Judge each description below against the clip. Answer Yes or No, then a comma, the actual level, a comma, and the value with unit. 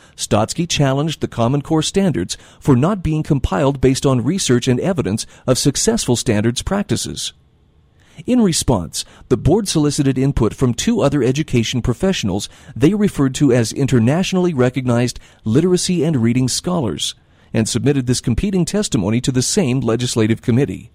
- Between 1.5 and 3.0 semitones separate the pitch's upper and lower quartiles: No, average, 4.7 semitones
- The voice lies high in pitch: No, low, 135 Hz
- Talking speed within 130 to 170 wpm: Yes, average, 145 wpm